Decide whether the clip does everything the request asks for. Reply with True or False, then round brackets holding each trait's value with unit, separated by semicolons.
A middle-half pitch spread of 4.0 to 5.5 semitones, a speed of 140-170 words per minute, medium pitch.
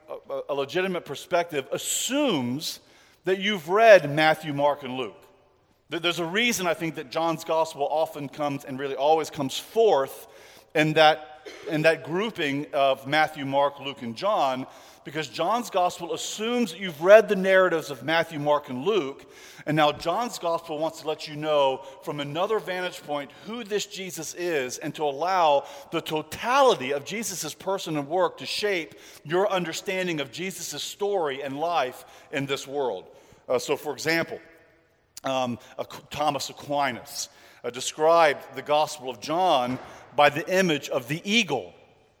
True (4.4 semitones; 155 wpm; 155 Hz)